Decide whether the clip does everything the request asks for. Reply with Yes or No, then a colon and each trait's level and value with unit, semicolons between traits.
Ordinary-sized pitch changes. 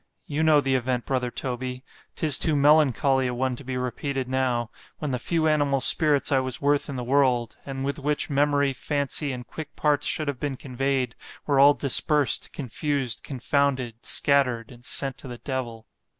No: narrow, 2.3 semitones